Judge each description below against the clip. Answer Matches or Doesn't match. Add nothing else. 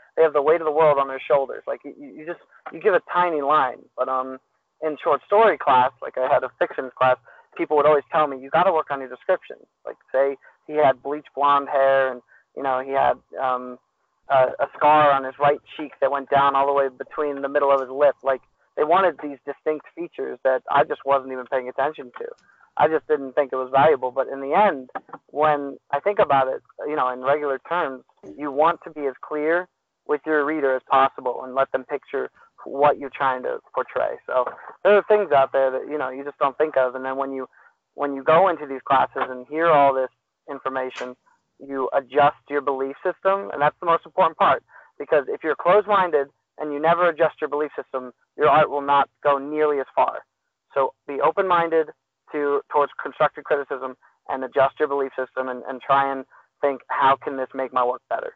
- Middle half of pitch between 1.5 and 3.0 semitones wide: Matches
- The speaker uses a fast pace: Matches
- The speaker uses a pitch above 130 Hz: Matches